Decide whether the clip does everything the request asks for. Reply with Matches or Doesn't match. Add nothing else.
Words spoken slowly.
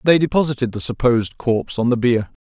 Doesn't match